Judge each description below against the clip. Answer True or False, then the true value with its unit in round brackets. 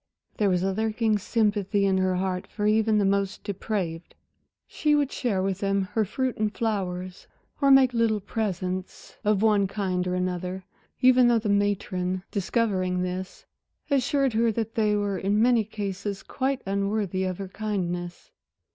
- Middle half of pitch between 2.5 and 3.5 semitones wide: True (2.8 semitones)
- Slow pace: False (160 wpm)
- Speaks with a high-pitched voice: True (200 Hz)